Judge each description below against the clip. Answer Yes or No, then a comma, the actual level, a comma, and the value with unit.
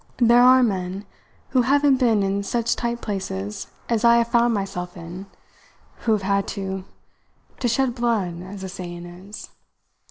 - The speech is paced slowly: No, average, 160 wpm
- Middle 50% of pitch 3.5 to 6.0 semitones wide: Yes, average, 4.1 semitones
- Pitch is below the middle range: No, high, 205 Hz